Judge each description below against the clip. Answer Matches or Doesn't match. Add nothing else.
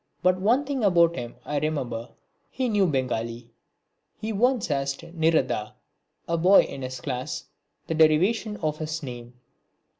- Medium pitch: Matches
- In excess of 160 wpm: Doesn't match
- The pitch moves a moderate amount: Doesn't match